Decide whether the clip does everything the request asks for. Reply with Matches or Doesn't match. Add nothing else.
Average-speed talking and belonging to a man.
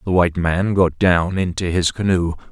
Matches